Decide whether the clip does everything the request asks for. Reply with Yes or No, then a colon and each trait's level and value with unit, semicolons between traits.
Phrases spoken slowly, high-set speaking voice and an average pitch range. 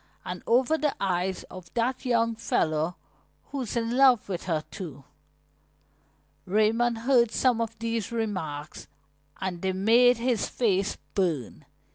Yes: slow, 130 wpm; high, 220 Hz; average, 4.6 semitones